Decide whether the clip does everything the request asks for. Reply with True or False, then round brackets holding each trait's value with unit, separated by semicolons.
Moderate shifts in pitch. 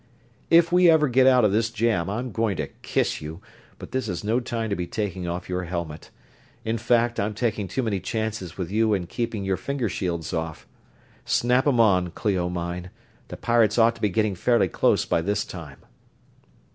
True (4.6 semitones)